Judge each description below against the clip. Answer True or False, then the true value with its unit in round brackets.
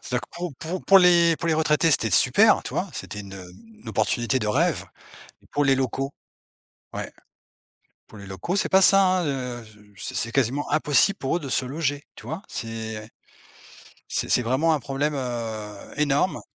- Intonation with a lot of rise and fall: True (5.8 semitones)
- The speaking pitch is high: False (135 Hz)